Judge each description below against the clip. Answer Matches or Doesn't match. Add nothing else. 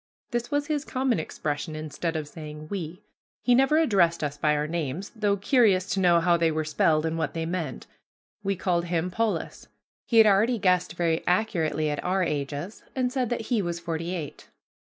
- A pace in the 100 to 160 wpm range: Doesn't match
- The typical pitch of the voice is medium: Matches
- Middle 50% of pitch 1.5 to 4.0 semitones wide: Doesn't match